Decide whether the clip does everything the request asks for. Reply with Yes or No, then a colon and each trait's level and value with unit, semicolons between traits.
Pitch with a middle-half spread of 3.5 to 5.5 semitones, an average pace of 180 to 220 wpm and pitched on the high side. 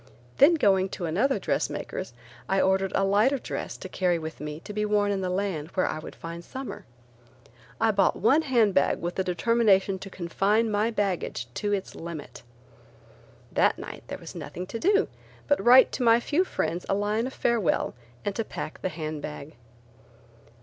Yes: average, 4.4 semitones; average, 185 wpm; high, 195 Hz